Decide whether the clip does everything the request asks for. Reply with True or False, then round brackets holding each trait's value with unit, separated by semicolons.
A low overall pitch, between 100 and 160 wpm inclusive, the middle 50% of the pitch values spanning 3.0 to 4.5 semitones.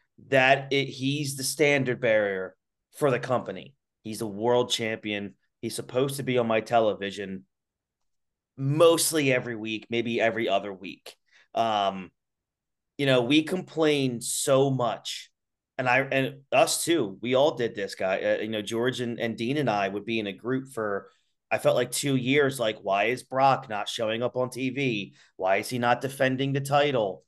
False (125 Hz; 175 wpm; 3.6 semitones)